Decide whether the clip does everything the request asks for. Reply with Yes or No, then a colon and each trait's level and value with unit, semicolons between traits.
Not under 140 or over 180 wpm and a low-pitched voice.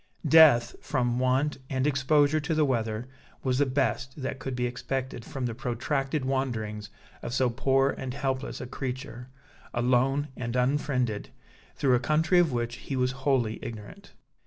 Yes: average, 160 wpm; low, 130 Hz